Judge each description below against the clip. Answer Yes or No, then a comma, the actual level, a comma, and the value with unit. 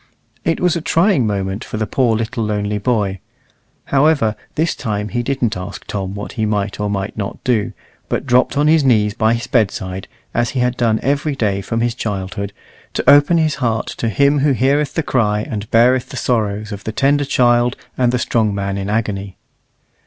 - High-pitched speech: No, low, 115 Hz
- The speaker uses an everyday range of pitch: Yes, average, 4.4 semitones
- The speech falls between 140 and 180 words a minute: No, average, 195 wpm